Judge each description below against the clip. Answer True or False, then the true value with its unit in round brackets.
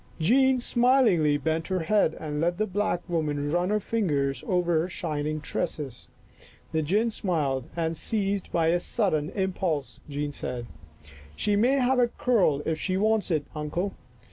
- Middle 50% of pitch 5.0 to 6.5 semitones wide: True (5.5 semitones)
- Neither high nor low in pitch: True (175 Hz)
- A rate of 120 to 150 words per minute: False (165 wpm)